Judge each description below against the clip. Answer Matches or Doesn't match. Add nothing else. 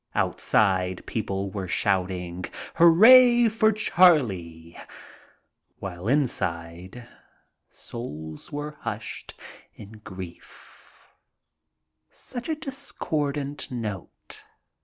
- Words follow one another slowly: Matches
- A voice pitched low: Matches